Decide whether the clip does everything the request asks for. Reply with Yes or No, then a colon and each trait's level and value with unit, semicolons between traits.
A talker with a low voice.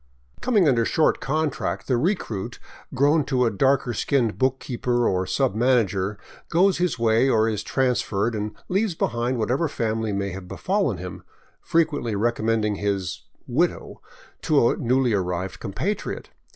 Yes: low, 120 Hz